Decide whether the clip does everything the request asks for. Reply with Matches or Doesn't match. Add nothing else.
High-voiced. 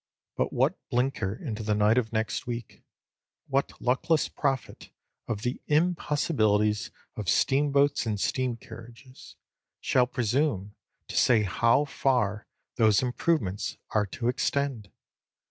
Doesn't match